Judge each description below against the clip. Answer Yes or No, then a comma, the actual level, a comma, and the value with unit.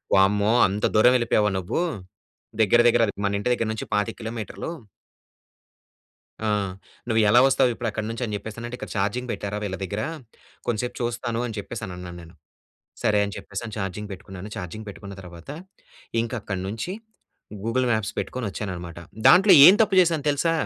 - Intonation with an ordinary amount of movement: Yes, average, 3.2 semitones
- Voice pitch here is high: No, low, 110 Hz